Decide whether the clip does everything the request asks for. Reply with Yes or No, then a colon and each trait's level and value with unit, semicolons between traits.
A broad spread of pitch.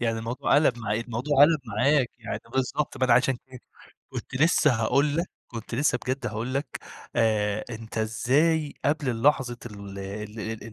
No: average, 4.2 semitones